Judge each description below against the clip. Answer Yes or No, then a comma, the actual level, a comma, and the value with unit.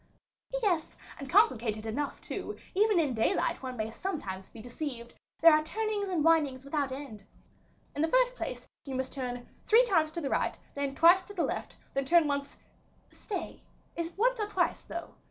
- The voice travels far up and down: Yes, wide, 6.3 semitones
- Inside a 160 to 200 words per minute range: Yes, average, 185 wpm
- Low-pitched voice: No, very high, 305 Hz